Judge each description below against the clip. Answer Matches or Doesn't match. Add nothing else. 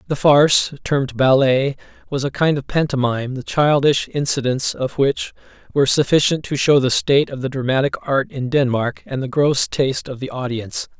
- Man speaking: Matches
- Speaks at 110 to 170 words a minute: Doesn't match